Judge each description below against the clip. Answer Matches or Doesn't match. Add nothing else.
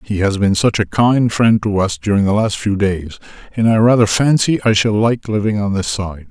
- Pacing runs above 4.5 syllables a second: Matches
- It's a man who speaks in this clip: Matches